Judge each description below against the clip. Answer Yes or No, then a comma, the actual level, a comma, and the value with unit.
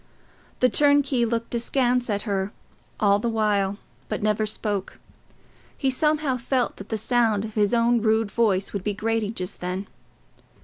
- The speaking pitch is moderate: No, high, 220 Hz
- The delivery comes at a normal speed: Yes, average, 160 wpm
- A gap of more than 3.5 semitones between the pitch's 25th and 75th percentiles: No, average, 3.0 semitones